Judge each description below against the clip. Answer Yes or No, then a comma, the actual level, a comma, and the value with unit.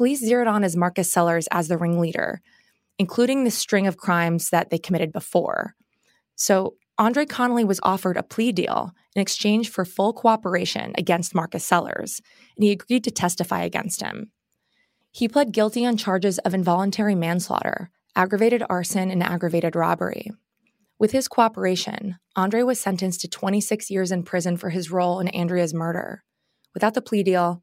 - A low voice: No, high, 190 Hz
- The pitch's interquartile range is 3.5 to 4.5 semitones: Yes, average, 3.9 semitones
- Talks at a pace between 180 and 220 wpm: No, average, 165 wpm